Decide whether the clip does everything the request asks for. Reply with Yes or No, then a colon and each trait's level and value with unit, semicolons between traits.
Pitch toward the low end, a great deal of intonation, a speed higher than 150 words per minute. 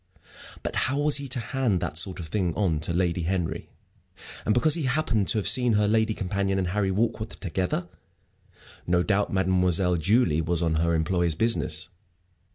No: very low, 95 Hz; average, 4.2 semitones; average, 175 wpm